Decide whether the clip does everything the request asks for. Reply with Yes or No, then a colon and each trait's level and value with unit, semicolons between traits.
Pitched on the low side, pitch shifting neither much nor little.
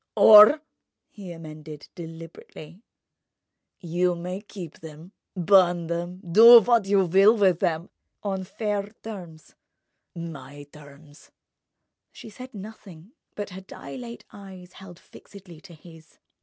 No: medium, 180 Hz; average, 3.7 semitones